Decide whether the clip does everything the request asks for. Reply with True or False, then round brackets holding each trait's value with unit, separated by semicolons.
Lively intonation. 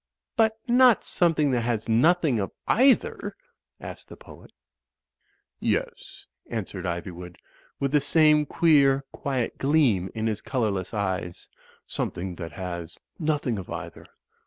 True (8.5 semitones)